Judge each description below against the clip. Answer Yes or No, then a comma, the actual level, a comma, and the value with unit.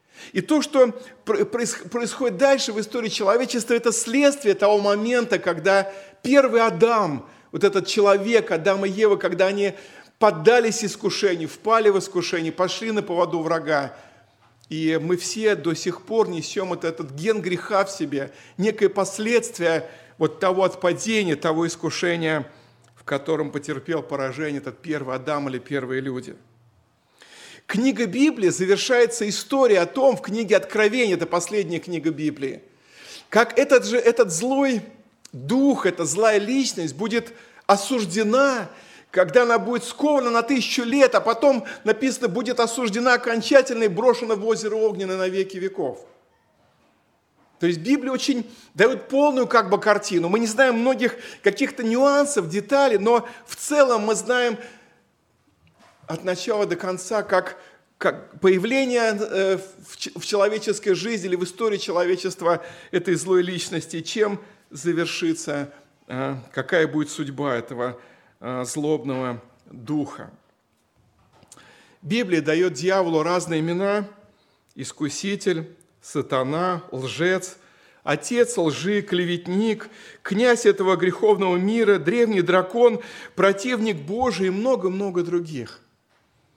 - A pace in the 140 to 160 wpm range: No, average, 120 wpm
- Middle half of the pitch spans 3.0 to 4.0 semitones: No, wide, 5.5 semitones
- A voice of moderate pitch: No, high, 195 Hz